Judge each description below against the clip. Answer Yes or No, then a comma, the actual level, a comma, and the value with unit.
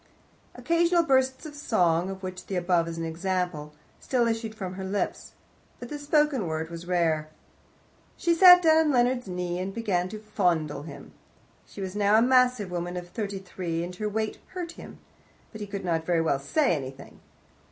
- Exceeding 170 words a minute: Yes, average, 185 wpm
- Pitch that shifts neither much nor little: No, wide, 6.2 semitones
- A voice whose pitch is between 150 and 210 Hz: Yes, high, 190 Hz